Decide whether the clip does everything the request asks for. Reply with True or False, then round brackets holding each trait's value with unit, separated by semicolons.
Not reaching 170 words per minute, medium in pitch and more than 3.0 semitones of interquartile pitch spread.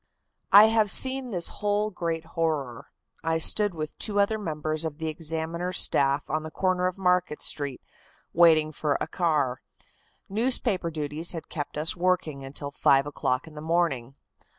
True (160 wpm; 165 Hz; 3.5 semitones)